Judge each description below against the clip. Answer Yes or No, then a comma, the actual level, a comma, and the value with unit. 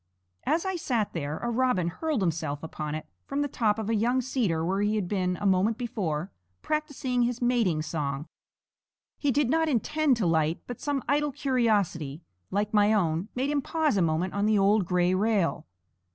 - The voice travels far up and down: Yes, wide, 6.7 semitones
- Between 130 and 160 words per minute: No, average, 190 wpm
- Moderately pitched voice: No, high, 210 Hz